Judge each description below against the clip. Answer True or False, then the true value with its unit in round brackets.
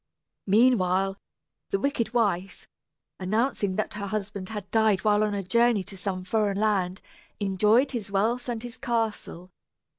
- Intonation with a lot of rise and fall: False (3.0 semitones)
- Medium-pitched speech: False (210 Hz)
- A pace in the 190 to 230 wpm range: False (145 wpm)